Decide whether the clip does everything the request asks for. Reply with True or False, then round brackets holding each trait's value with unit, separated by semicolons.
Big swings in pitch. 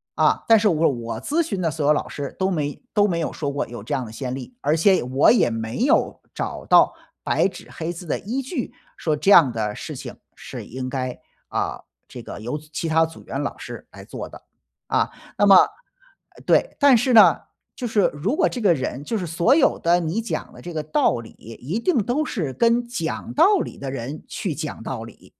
True (8.8 semitones)